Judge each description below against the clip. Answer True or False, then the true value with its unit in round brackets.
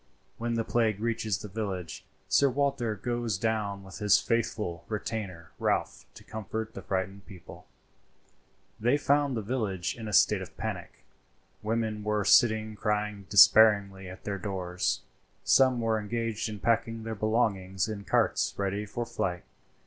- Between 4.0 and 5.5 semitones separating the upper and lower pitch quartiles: False (2.5 semitones)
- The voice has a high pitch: False (105 Hz)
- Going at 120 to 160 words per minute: True (150 wpm)